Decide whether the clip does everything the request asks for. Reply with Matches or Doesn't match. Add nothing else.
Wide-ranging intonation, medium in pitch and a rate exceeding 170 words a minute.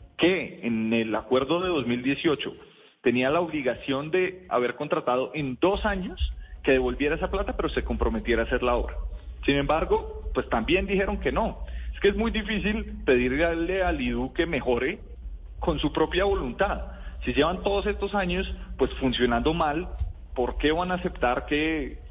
Doesn't match